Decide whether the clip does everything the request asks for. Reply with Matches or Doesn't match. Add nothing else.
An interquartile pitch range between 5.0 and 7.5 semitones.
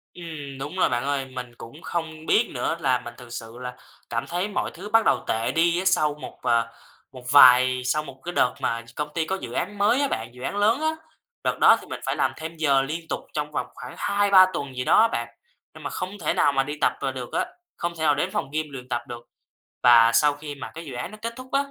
Matches